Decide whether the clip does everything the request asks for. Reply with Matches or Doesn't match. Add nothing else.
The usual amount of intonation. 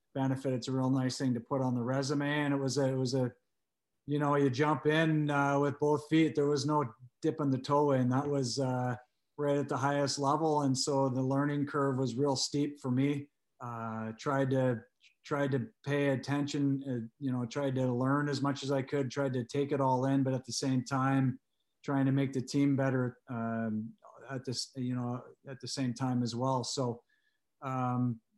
Doesn't match